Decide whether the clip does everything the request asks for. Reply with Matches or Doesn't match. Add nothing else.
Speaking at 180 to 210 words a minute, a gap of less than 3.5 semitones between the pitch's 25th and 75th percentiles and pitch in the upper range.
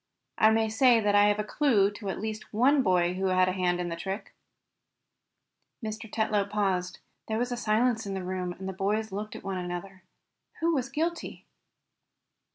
Matches